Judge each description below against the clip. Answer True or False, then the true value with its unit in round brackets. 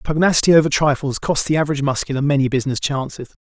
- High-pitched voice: False (140 Hz)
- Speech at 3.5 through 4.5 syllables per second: False (7.3 syllables/s)